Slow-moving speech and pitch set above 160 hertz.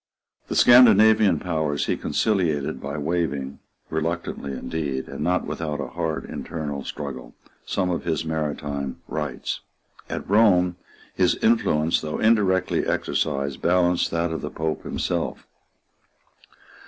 No: slow, 120 wpm; very low, 80 Hz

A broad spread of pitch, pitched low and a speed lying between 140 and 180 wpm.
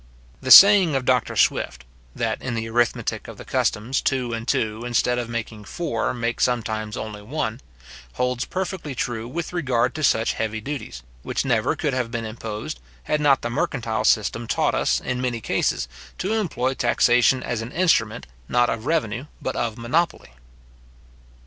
No: average, 3.0 semitones; low, 120 Hz; average, 170 wpm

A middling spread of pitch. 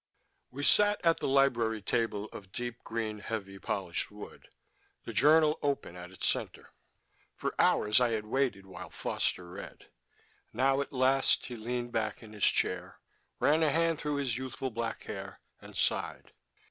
Yes: average, 4.4 semitones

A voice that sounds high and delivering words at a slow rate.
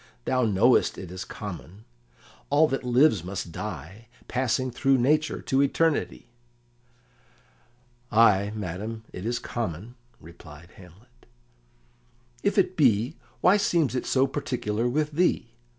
No: low, 120 Hz; slow, 120 wpm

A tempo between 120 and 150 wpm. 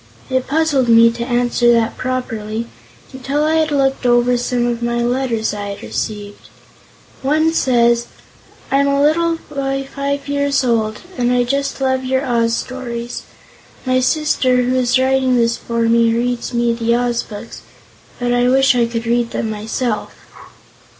No: average, 160 wpm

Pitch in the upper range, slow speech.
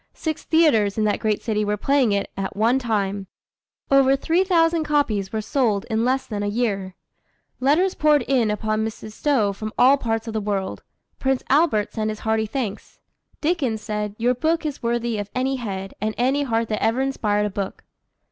No: high, 225 Hz; average, 195 wpm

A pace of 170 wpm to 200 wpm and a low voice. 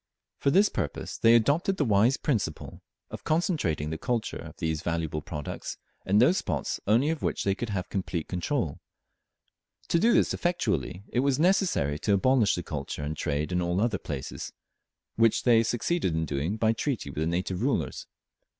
Yes: average, 175 wpm; low, 100 Hz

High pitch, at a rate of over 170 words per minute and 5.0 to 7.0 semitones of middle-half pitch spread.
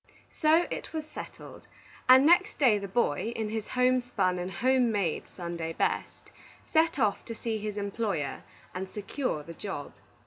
No: high, 215 Hz; average, 165 wpm; wide, 5.5 semitones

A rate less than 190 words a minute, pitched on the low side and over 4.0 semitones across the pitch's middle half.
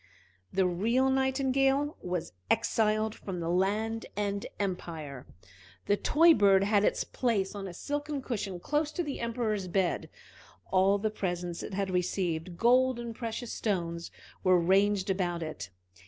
No: average, 145 wpm; high, 200 Hz; average, 4.7 semitones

